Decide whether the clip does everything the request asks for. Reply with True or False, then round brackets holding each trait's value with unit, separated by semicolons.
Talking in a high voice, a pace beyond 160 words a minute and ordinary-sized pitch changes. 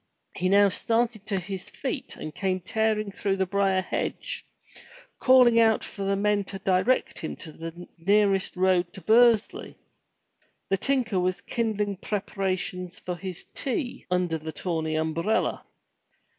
False (195 Hz; 140 wpm; 3.1 semitones)